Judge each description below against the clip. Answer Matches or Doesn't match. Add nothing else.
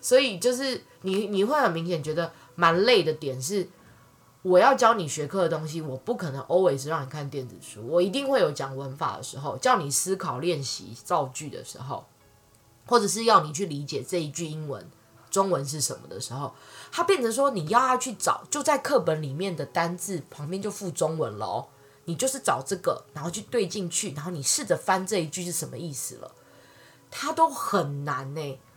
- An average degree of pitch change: Doesn't match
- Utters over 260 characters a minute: Matches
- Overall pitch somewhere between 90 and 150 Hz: Doesn't match